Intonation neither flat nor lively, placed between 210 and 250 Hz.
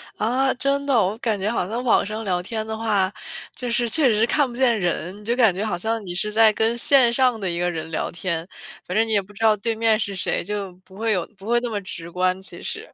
Yes: average, 3.7 semitones; high, 215 Hz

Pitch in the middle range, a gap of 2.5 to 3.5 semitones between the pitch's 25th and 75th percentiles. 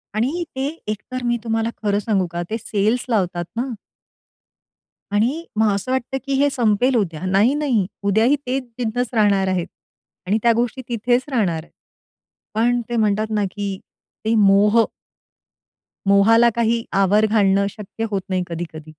No: high, 215 Hz; average, 3.2 semitones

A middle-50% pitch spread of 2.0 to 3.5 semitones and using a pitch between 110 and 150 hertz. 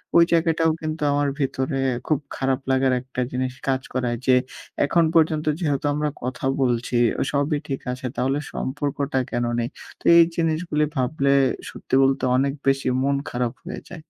Yes: average, 2.8 semitones; low, 135 Hz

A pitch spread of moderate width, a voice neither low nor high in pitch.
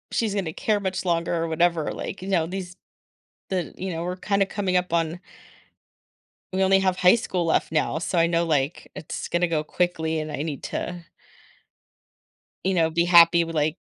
No: narrow, 2.3 semitones; medium, 175 Hz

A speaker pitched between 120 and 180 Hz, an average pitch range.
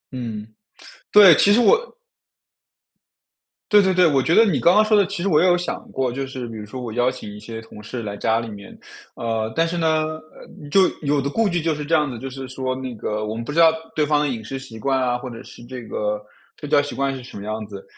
No: low, 135 Hz; wide, 6.2 semitones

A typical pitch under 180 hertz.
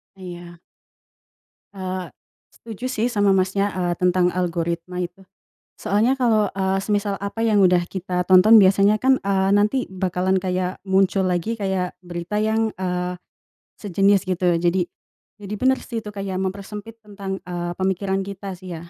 No: high, 190 Hz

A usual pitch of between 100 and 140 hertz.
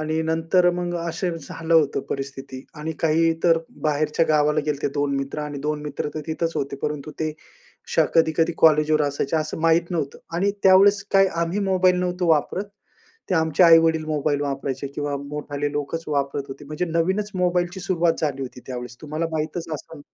No: medium, 155 Hz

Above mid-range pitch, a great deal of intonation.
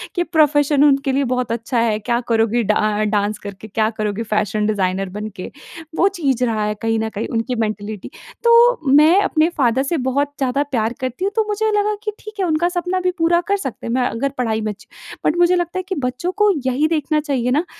Yes: very high, 260 Hz; wide, 7.7 semitones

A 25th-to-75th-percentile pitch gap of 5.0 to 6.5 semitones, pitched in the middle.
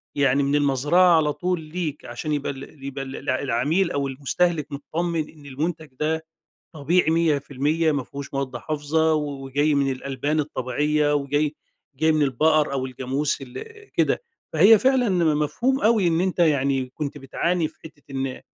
No: average, 2.7 semitones; medium, 150 Hz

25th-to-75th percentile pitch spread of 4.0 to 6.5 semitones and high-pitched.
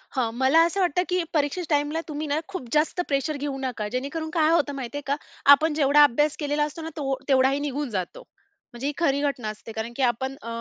No: average, 2.8 semitones; very high, 285 Hz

